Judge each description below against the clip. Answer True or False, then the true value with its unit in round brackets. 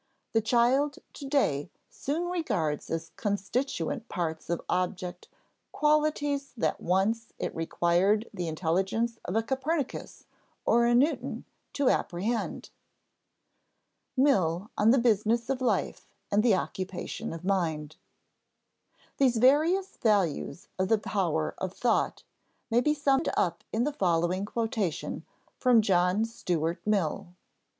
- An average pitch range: False (6.2 semitones)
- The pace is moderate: False (125 wpm)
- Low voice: False (215 Hz)